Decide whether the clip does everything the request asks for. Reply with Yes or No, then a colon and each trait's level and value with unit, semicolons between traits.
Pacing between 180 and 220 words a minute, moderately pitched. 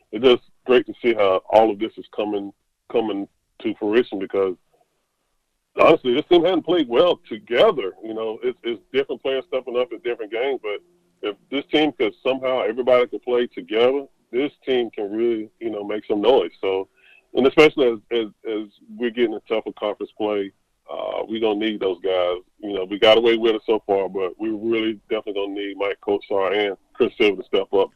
Yes: fast, 205 wpm; medium, 145 Hz